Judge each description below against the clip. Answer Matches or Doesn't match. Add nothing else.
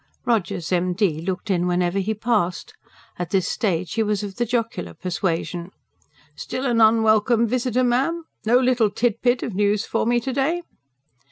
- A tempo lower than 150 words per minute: Doesn't match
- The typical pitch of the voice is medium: Doesn't match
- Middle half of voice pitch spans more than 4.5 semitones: Matches